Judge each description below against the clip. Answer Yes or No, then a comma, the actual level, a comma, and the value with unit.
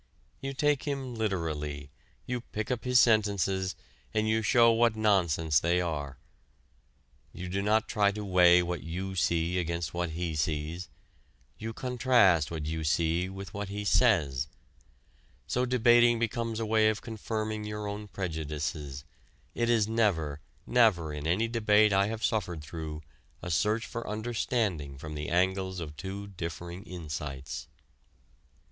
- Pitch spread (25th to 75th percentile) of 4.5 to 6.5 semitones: Yes, average, 5.2 semitones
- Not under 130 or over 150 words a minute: Yes, average, 145 wpm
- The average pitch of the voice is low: Yes, very low, 95 Hz